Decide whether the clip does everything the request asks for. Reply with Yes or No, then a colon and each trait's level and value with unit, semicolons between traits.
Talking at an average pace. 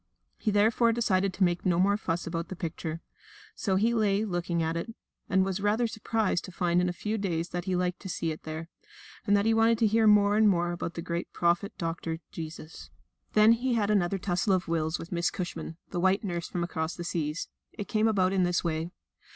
No: fast, 225 wpm